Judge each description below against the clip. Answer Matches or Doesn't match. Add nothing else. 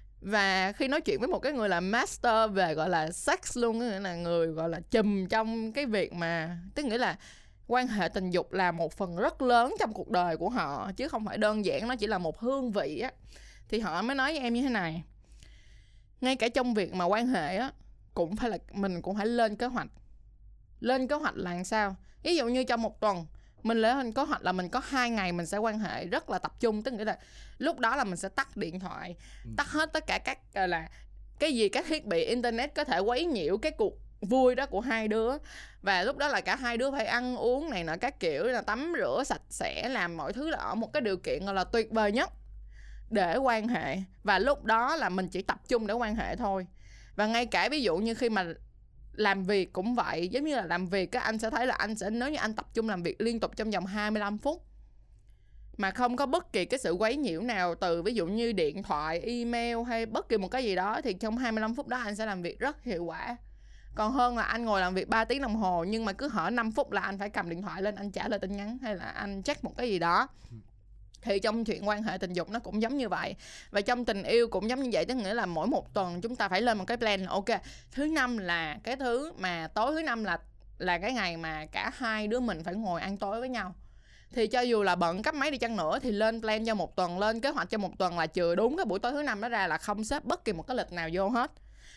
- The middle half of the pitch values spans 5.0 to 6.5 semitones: Doesn't match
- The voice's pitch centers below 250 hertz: Matches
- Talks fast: Matches